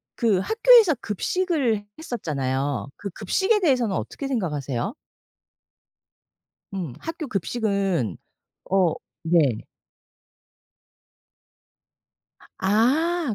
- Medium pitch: No, high, 210 Hz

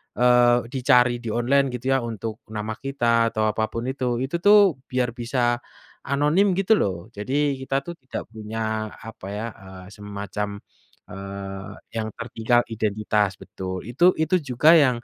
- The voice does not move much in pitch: No, average, 3.9 semitones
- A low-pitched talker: Yes, low, 120 Hz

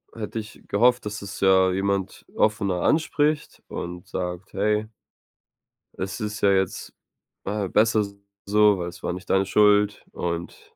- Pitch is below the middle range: Yes, low, 100 Hz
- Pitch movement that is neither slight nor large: No, narrow, 2.1 semitones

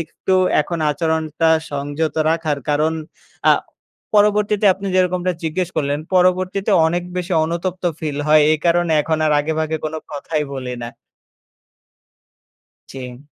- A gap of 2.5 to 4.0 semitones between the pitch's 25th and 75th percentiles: Yes, average, 3.3 semitones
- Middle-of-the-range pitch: Yes, medium, 160 Hz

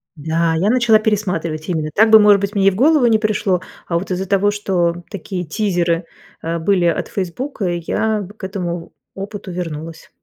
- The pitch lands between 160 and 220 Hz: Yes, high, 190 Hz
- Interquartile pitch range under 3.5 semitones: No, average, 3.8 semitones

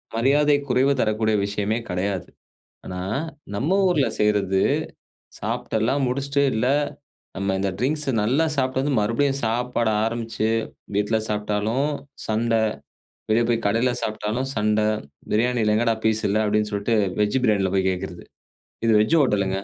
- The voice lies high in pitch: No, low, 110 Hz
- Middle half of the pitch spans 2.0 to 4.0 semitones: Yes, average, 3.4 semitones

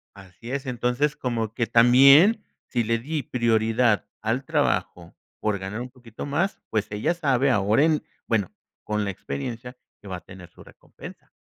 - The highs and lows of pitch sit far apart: No, average, 4.5 semitones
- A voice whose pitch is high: No, low, 120 Hz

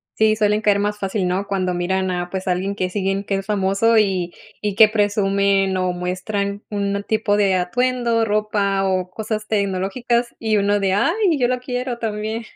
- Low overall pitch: No, high, 200 Hz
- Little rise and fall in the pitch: Yes, narrow, 2.3 semitones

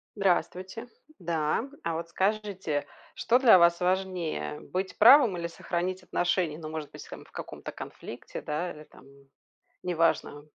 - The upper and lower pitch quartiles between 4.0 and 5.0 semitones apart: No, average, 2.9 semitones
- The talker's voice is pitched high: No, medium, 175 Hz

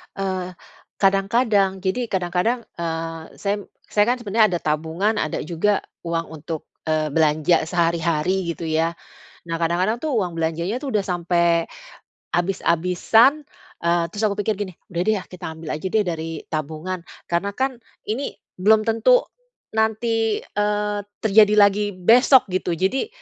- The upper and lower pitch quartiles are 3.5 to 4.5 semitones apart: Yes, average, 4.2 semitones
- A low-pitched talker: No, medium, 185 Hz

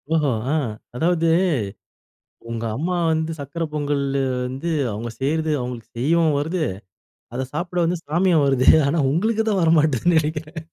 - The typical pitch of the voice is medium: Yes, medium, 160 Hz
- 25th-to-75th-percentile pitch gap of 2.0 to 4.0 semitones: Yes, average, 3.2 semitones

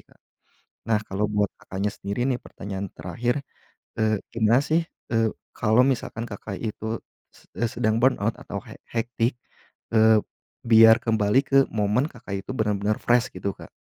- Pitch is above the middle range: No, low, 110 Hz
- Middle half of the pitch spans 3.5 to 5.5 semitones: No, narrow, 2.6 semitones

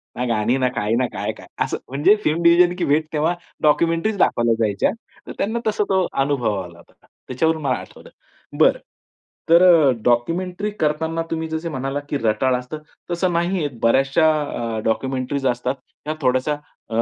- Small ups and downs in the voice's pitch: No, average, 5.0 semitones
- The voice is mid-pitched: Yes, medium, 145 Hz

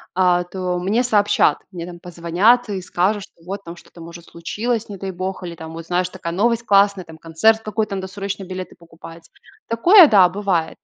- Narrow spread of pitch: No, average, 3.2 semitones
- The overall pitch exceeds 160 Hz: Yes, medium, 185 Hz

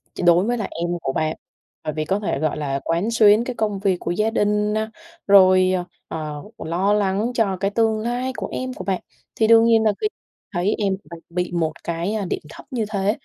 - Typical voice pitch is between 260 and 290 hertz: No, high, 200 Hz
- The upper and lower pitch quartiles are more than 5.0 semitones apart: No, average, 4.1 semitones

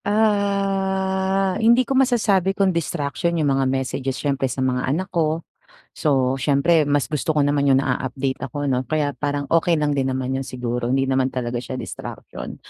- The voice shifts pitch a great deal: Yes, wide, 6.0 semitones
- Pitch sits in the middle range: Yes, medium, 145 Hz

